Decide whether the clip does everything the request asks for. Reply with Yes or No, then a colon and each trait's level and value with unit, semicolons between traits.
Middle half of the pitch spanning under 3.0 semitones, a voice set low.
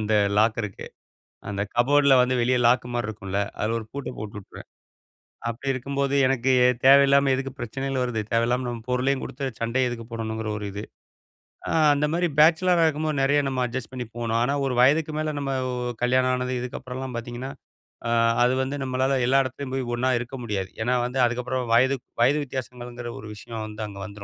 Yes: narrow, 2.6 semitones; low, 125 Hz